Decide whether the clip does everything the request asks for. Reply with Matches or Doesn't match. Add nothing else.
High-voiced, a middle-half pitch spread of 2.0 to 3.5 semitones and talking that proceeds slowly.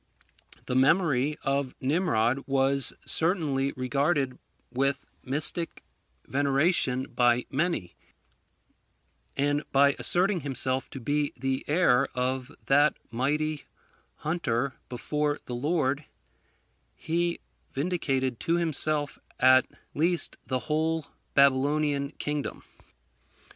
Doesn't match